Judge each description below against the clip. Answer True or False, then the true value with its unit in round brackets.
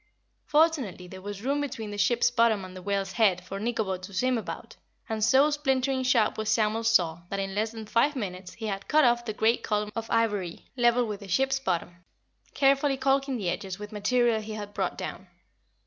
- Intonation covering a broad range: False (4.2 semitones)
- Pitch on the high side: True (220 Hz)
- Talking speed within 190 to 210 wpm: True (205 wpm)